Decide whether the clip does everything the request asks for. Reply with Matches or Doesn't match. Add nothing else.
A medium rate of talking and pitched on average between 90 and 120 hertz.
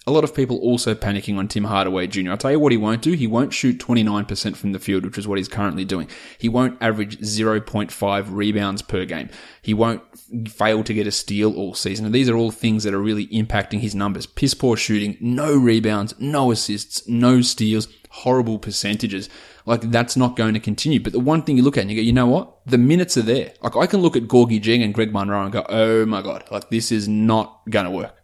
Doesn't match